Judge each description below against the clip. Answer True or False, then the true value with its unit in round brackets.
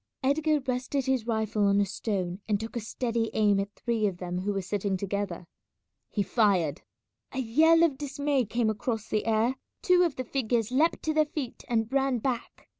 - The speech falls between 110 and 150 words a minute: False (190 wpm)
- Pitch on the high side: True (230 Hz)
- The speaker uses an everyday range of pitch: True (4.7 semitones)